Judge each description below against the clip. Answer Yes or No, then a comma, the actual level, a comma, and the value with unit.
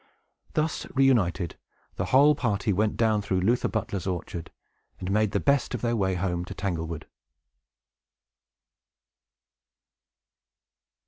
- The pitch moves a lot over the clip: No, average, 4.5 semitones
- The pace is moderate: No, slow, 115 wpm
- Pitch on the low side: Yes, low, 100 Hz